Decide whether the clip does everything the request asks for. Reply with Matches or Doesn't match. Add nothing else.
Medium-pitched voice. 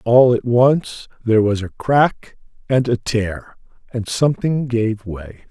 Doesn't match